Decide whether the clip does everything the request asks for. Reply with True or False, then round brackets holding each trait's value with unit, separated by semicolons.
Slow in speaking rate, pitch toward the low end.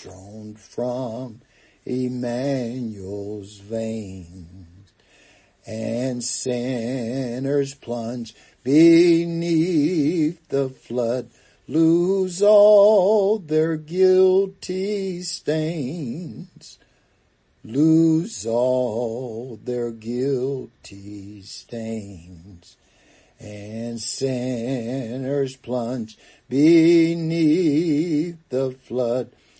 True (55 wpm; 130 Hz)